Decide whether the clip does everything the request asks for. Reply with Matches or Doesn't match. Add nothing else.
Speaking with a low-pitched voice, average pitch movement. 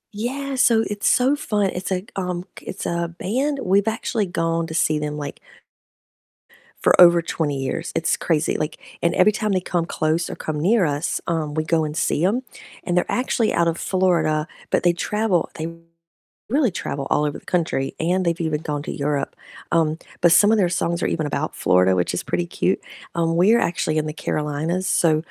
Doesn't match